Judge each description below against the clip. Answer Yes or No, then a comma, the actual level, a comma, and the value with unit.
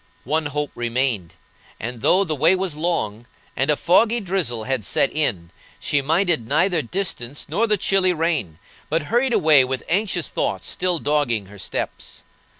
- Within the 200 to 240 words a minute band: No, average, 160 wpm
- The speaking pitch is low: No, medium, 150 Hz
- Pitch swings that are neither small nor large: No, wide, 6.6 semitones